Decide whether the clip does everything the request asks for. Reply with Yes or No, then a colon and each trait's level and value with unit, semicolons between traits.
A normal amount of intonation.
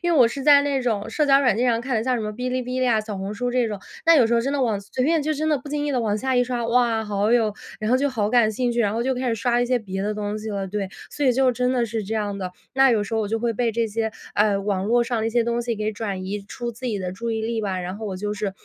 Yes: average, 3.2 semitones